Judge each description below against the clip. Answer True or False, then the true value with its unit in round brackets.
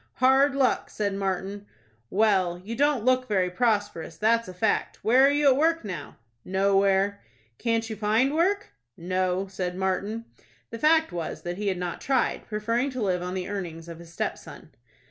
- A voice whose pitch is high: True (205 Hz)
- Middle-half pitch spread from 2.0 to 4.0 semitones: False (5.2 semitones)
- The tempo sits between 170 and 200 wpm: True (175 wpm)